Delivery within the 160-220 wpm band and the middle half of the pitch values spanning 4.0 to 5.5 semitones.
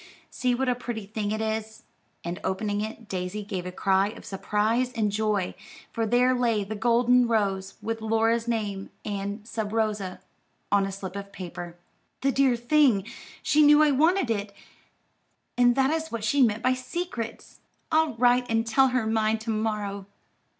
No: average, 170 wpm; average, 3.2 semitones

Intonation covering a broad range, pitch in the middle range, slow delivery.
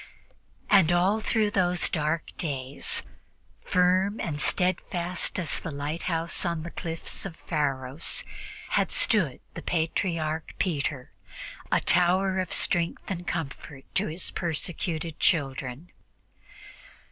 No: average, 3.0 semitones; medium, 170 Hz; slow, 110 wpm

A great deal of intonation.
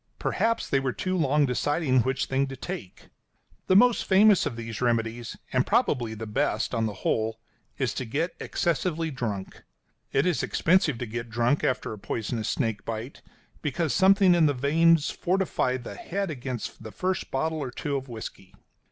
Yes: wide, 6.1 semitones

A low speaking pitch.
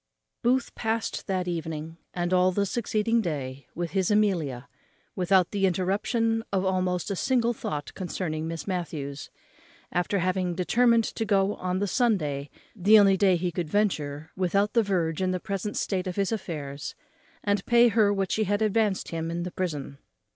No: medium, 185 Hz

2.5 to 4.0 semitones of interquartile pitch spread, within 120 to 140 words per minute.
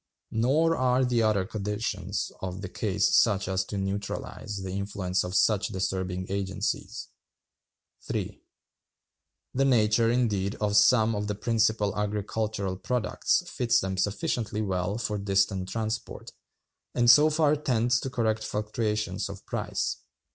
Yes: average, 2.9 semitones; slow, 135 wpm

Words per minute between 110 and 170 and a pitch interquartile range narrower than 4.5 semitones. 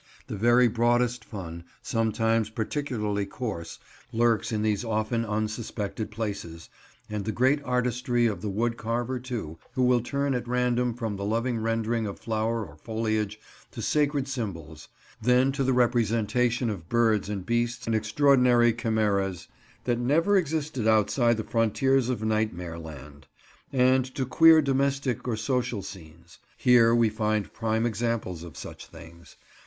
Yes: average, 150 wpm; average, 2.7 semitones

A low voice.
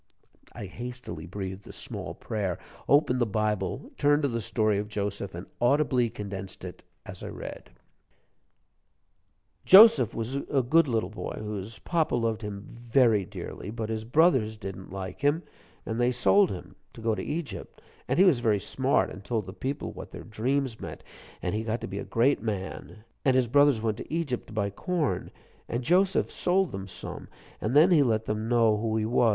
Yes: low, 115 Hz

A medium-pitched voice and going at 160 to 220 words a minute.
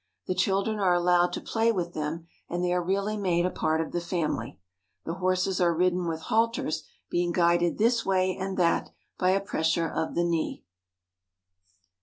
Yes: medium, 180 Hz; average, 180 wpm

